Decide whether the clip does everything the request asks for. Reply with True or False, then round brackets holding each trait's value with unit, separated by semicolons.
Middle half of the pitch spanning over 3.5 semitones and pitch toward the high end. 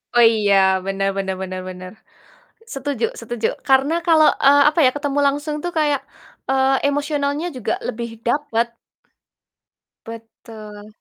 True (4.9 semitones; 255 Hz)